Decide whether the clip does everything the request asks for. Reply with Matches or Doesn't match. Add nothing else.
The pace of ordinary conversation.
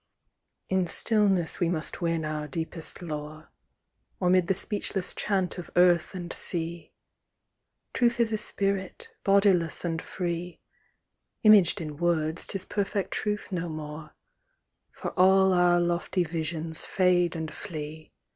Doesn't match